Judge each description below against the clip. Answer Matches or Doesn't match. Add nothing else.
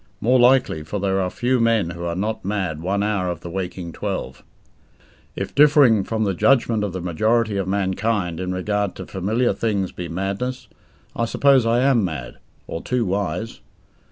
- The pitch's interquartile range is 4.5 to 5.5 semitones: Doesn't match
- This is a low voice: Matches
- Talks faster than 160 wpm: Matches